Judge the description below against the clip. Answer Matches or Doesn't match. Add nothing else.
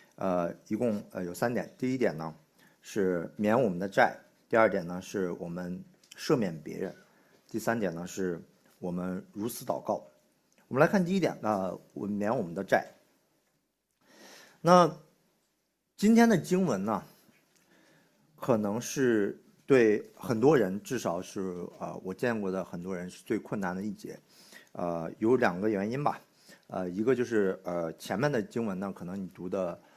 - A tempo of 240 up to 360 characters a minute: Doesn't match